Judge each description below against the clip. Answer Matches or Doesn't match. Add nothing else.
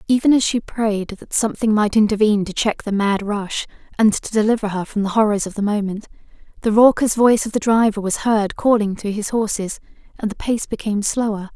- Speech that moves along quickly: Matches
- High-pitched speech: Matches